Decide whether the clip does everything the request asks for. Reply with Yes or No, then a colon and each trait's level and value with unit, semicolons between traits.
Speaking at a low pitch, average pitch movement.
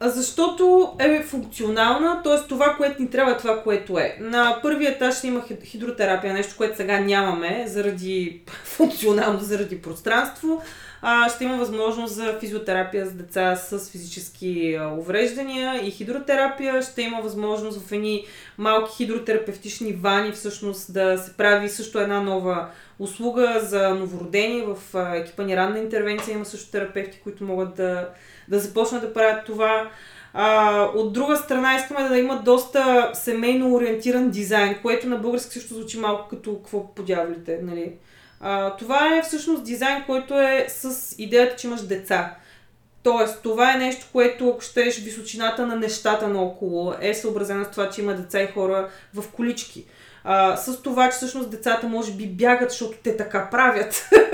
No: high, 220 Hz; average, 3.7 semitones